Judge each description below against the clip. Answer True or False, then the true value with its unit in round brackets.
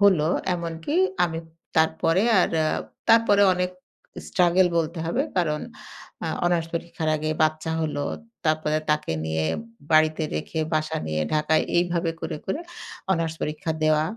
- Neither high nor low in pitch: True (160 Hz)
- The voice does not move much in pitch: True (2.0 semitones)